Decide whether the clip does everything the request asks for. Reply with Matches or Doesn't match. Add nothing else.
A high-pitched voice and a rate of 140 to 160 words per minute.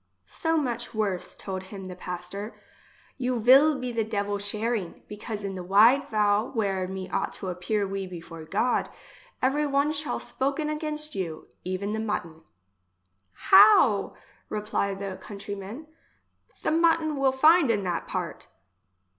Matches